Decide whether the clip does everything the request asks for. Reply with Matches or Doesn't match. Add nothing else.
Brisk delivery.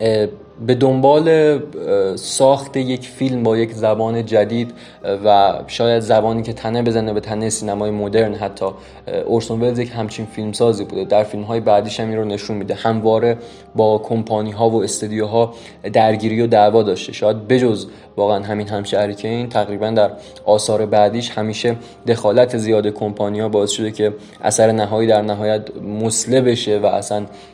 Matches